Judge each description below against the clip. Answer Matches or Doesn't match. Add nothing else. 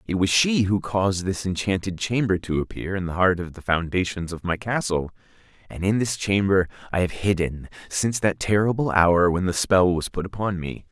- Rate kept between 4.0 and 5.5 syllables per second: Matches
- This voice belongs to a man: Matches